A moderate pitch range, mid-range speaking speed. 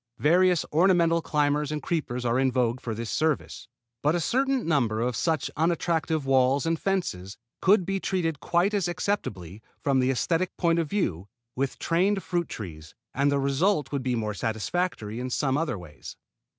No: wide, 5.9 semitones; average, 175 wpm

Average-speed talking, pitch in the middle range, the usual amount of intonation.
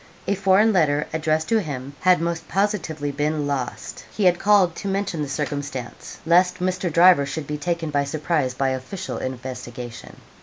Yes: average, 165 wpm; medium, 155 Hz; average, 4.4 semitones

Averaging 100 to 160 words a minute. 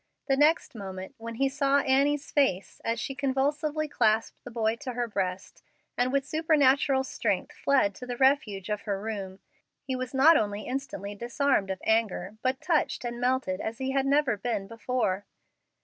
No: average, 175 wpm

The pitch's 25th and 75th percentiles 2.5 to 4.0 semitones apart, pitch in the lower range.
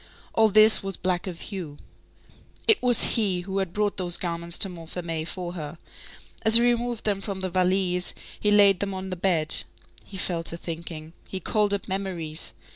No: average, 2.9 semitones; medium, 185 Hz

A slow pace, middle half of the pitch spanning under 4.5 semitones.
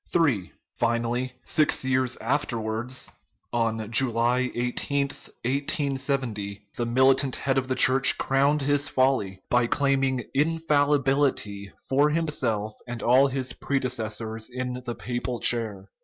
Yes: slow, 115 wpm; average, 2.9 semitones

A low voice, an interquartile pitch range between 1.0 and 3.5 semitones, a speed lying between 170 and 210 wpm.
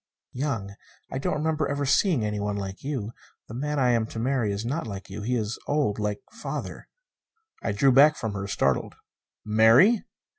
No: low, 115 Hz; wide, 5.6 semitones; average, 185 wpm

